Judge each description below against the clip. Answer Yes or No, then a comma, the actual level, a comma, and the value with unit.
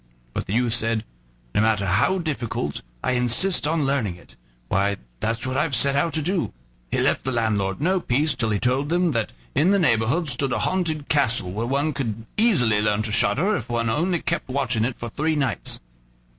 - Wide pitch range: Yes, wide, 5.7 semitones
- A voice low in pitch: Yes, low, 130 Hz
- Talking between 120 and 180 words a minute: No, fast, 205 wpm